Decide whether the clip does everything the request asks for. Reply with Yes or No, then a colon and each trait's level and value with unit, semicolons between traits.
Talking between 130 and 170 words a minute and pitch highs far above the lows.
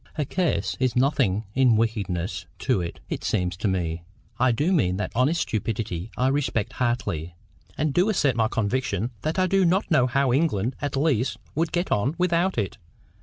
No: average, 180 wpm; wide, 7.0 semitones